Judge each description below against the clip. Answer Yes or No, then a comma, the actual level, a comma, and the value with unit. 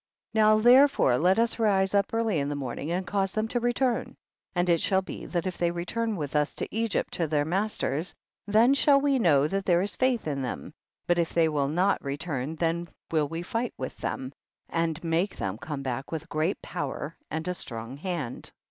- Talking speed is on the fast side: Yes, fast, 215 wpm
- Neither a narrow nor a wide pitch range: No, wide, 6.1 semitones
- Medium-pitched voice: Yes, medium, 175 Hz